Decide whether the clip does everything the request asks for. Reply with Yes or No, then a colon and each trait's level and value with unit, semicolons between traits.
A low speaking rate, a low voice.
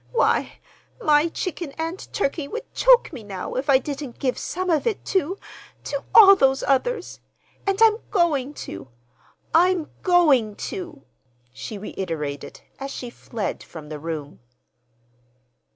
No: slow, 130 wpm; very high, 285 Hz